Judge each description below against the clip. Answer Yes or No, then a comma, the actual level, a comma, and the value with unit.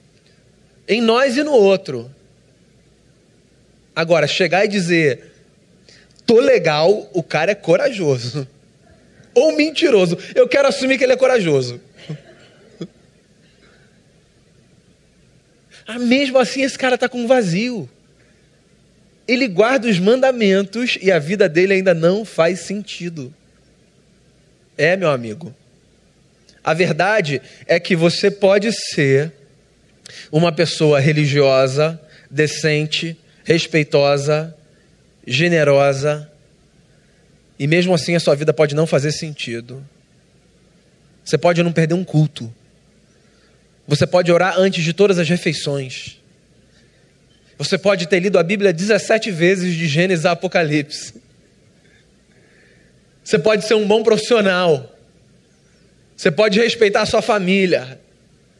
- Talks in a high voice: No, medium, 175 Hz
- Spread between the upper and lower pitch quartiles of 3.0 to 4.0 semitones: No, wide, 5.4 semitones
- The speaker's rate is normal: No, slow, 110 wpm